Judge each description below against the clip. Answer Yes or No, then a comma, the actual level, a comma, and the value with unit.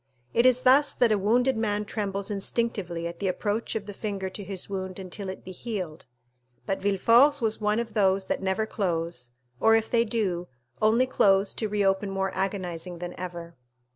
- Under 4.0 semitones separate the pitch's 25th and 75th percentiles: Yes, average, 2.9 semitones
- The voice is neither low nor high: No, high, 200 Hz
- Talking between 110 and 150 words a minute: No, average, 185 wpm